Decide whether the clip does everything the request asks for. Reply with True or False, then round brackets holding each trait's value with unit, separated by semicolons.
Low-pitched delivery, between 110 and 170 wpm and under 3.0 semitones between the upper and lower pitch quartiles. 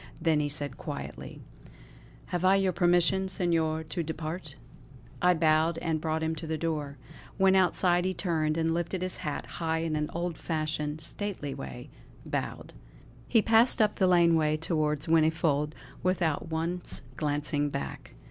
False (160 Hz; 150 wpm; 2.4 semitones)